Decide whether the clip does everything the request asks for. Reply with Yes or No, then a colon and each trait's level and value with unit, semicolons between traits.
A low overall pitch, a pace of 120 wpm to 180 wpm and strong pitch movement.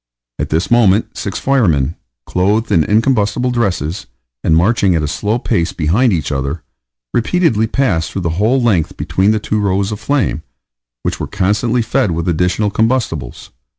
Yes: low, 100 Hz; average, 165 wpm; wide, 5.7 semitones